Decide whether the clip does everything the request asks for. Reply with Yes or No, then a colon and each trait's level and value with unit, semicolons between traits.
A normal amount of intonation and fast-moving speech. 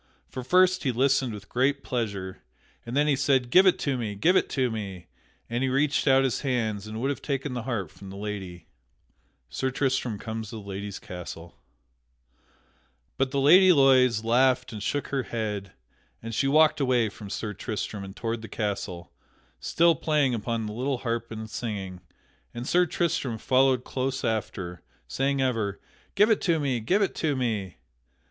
No: average, 4.4 semitones; average, 180 wpm